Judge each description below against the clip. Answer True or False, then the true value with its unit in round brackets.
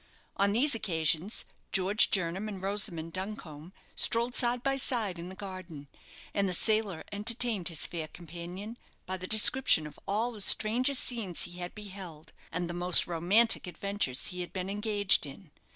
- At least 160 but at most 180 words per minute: True (165 wpm)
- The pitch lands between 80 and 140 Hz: False (195 Hz)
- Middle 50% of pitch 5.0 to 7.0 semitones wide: False (3.8 semitones)